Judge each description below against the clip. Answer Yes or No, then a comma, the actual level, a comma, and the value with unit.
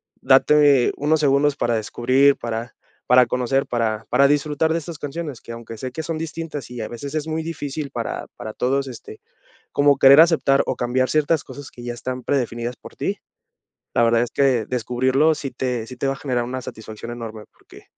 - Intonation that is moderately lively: Yes, average, 3.4 semitones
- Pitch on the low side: Yes, low, 130 Hz